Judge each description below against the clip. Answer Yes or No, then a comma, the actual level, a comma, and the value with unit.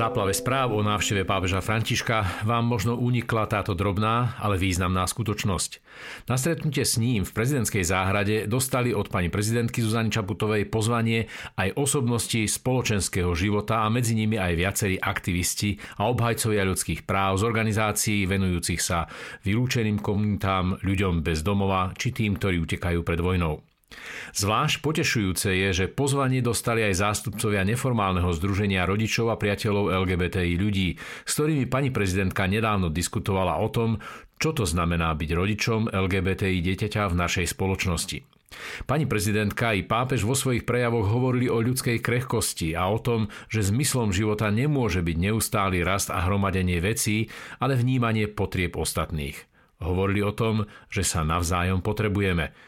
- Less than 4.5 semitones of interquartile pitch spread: Yes, average, 3.6 semitones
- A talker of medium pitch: No, low, 105 Hz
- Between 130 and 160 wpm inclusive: Yes, average, 140 wpm